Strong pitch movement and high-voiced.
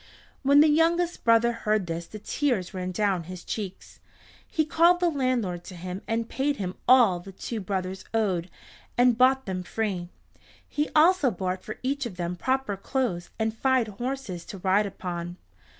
Yes: wide, 6.2 semitones; high, 215 Hz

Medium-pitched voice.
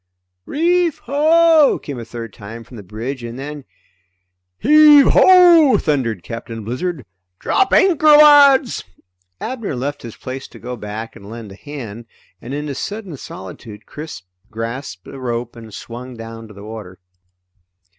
No: low, 130 Hz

